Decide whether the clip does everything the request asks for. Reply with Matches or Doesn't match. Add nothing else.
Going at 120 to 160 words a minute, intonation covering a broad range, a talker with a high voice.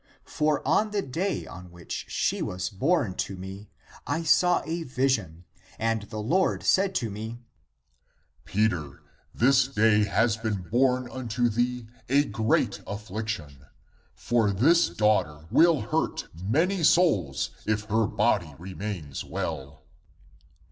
Doesn't match